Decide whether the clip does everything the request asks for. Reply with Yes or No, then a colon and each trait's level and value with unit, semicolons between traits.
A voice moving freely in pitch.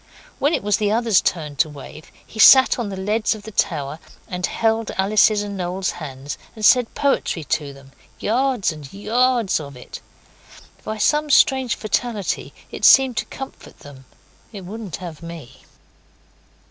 Yes: wide, 6.4 semitones